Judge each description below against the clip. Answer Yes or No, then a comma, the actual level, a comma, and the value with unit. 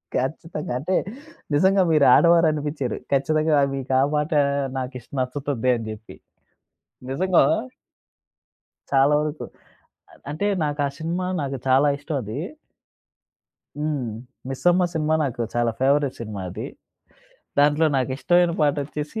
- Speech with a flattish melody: No, average, 3.0 semitones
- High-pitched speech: No, medium, 145 Hz